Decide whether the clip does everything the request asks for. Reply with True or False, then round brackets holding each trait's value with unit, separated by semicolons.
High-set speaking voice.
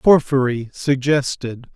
False (135 Hz)